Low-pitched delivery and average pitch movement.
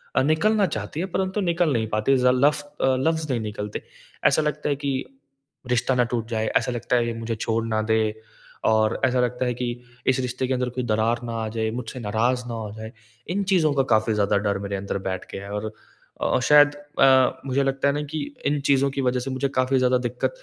Yes: low, 125 Hz; average, 3.9 semitones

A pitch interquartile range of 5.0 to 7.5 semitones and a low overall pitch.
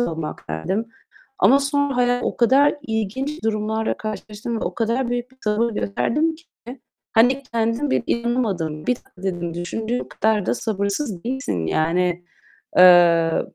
No: average, 5.3 semitones; high, 220 Hz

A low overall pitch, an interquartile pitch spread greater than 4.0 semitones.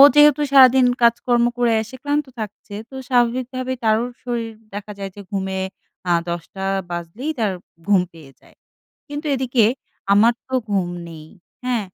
No: high, 235 Hz; average, 4.5 semitones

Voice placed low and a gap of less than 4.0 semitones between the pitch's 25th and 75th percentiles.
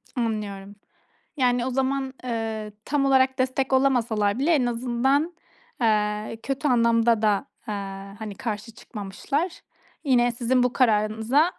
No: high, 240 Hz; average, 3.4 semitones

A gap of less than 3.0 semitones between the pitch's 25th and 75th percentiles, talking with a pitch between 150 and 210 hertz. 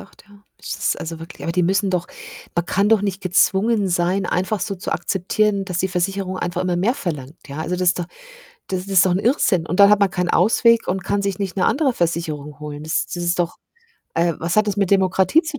Yes: narrow, 2.5 semitones; medium, 185 Hz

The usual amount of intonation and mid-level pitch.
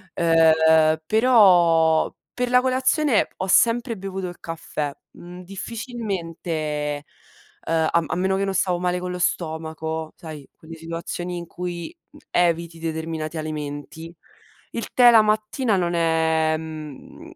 Yes: average, 3.3 semitones; medium, 170 Hz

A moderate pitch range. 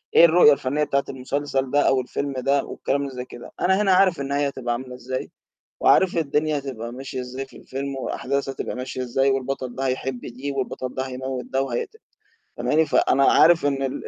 No: narrow, 1.8 semitones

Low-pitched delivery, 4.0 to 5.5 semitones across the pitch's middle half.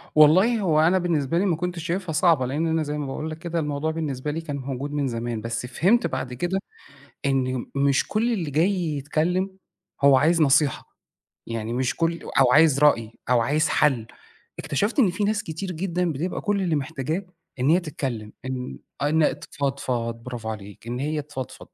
No: medium, 150 Hz; average, 4.5 semitones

